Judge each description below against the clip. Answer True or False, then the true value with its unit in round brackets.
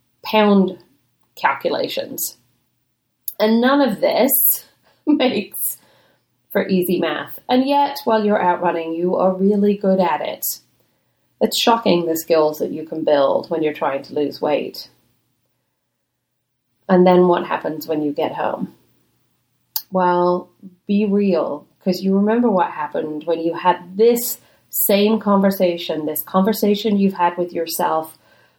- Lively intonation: False (4.5 semitones)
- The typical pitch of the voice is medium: True (180 Hz)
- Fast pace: False (135 wpm)